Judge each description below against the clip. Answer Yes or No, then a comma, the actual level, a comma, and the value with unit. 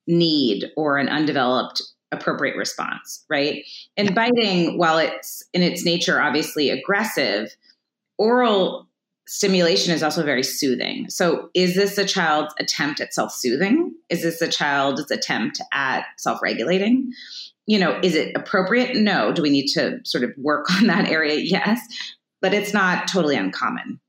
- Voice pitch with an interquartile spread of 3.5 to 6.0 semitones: Yes, average, 5.1 semitones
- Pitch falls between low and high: Yes, medium, 180 Hz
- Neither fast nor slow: Yes, average, 150 wpm